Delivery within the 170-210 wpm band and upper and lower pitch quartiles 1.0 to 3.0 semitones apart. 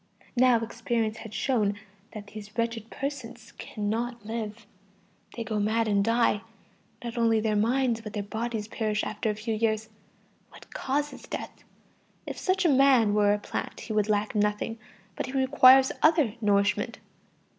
No: average, 155 wpm; narrow, 2.4 semitones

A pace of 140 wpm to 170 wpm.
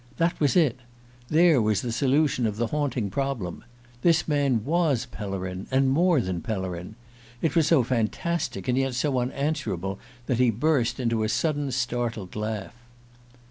Yes: average, 155 wpm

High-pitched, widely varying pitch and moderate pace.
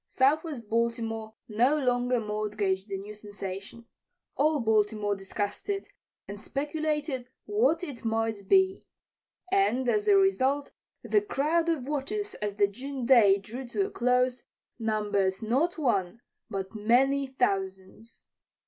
No: high, 240 Hz; wide, 5.8 semitones; slow, 130 wpm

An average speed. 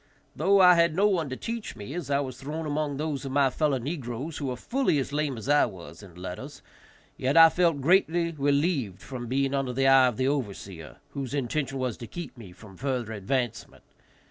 No: fast, 210 wpm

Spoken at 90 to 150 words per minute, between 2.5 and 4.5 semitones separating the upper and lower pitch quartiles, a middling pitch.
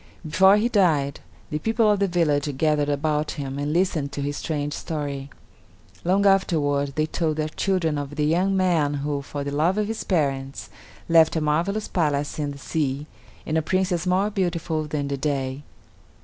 No: average, 180 wpm; average, 4.0 semitones; medium, 155 Hz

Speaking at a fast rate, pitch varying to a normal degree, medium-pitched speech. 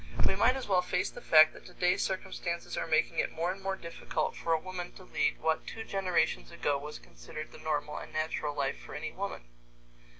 Yes: fast, 210 wpm; average, 3.5 semitones; medium, 170 Hz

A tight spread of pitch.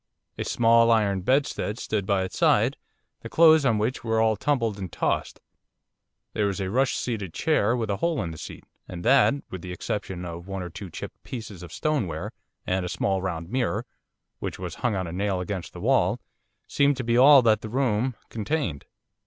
No: average, 4.9 semitones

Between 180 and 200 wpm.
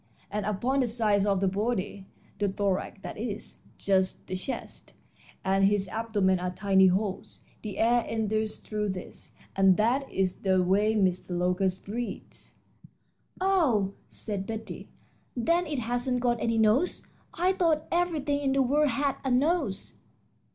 No: average, 150 wpm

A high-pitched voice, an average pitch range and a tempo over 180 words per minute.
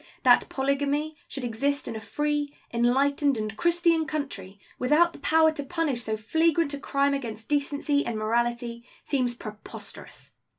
No: very high, 280 Hz; average, 4.0 semitones; average, 145 wpm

